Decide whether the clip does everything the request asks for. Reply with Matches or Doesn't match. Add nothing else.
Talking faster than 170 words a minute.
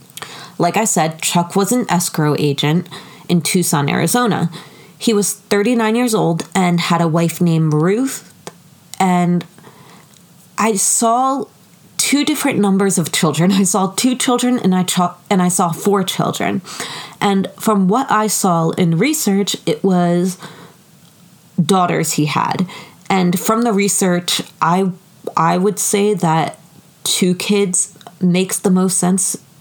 Doesn't match